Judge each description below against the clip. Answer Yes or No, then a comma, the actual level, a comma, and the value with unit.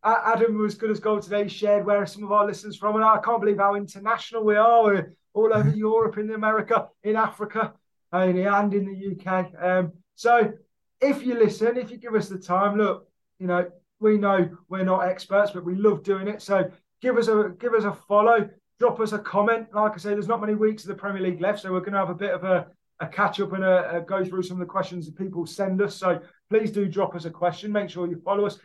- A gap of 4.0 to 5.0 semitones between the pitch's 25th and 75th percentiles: No, narrow, 2.5 semitones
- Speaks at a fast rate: Yes, fast, 260 wpm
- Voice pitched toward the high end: Yes, high, 205 Hz